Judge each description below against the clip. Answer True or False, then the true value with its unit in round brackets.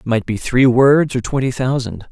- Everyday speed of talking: False (225 wpm)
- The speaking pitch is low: True (125 Hz)